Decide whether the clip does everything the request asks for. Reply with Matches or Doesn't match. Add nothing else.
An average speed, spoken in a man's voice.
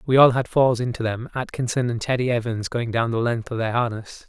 Doesn't match